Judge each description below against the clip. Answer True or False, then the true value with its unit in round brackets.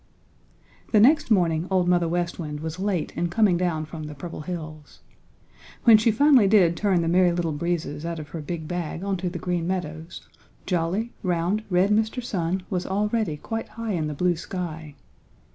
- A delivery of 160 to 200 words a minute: True (180 wpm)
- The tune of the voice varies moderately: True (3.3 semitones)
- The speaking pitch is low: False (175 Hz)